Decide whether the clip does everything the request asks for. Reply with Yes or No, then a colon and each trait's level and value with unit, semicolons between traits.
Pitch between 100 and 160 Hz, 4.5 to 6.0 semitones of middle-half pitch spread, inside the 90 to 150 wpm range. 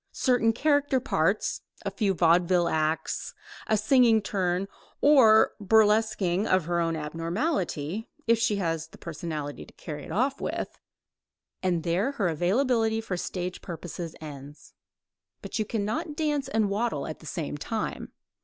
No: high, 195 Hz; average, 5.2 semitones; average, 145 wpm